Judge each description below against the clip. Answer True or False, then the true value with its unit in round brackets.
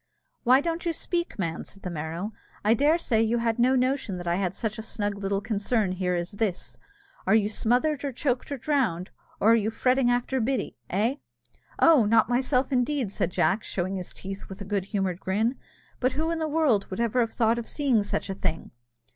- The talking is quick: True (215 wpm)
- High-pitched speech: True (225 Hz)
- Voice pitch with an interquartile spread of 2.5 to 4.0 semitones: False (4.8 semitones)